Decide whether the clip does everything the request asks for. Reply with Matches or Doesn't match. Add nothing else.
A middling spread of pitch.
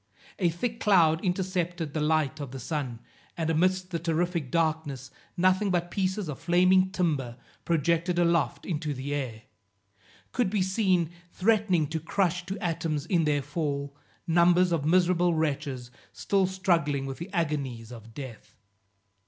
Matches